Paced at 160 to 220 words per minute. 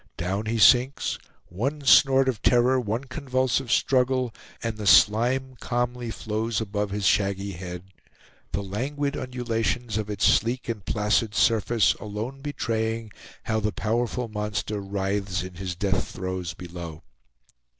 No: slow, 135 wpm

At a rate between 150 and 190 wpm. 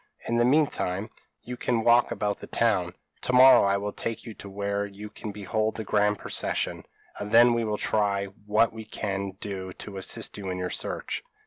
No: fast, 205 wpm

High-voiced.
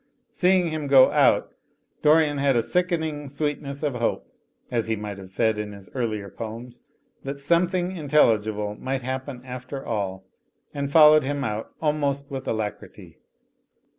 No: low, 135 Hz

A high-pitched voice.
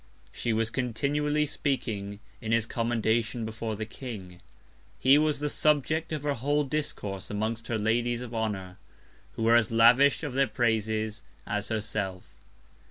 No: low, 115 Hz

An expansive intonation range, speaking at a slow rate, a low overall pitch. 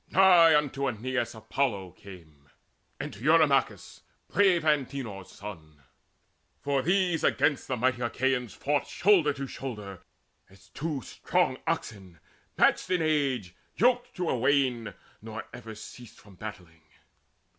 Yes: wide, 6.8 semitones; slow, 130 wpm; low, 130 Hz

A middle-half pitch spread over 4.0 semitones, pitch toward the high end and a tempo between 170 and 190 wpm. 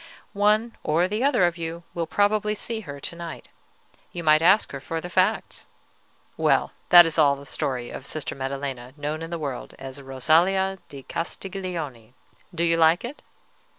No: average, 4.7 semitones; medium, 165 Hz; average, 175 wpm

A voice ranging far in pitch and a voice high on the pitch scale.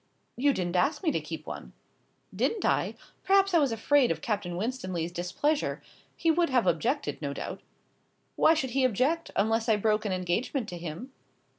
Yes: wide, 7.9 semitones; high, 235 Hz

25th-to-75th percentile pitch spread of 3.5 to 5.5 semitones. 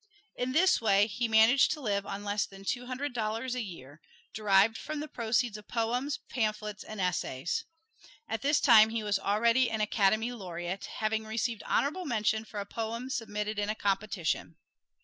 No: average, 3.0 semitones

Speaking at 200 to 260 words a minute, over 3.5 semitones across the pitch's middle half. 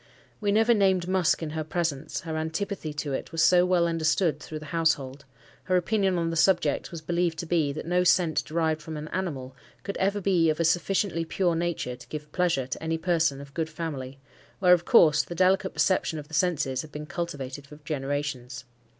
No: fast, 205 wpm; average, 3.0 semitones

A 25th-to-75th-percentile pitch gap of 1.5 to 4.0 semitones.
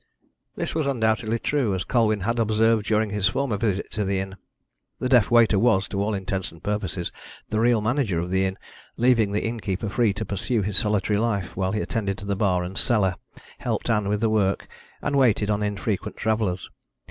Yes: average, 2.7 semitones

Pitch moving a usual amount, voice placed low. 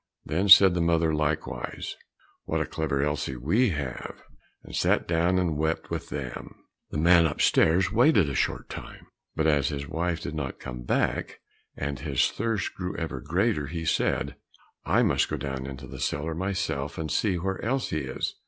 Yes: average, 4.0 semitones; very low, 80 Hz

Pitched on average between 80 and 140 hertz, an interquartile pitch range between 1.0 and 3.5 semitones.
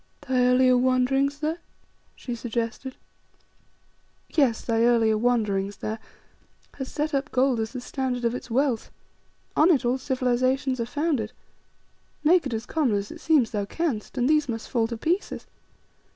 No: very high, 250 Hz; average, 3.2 semitones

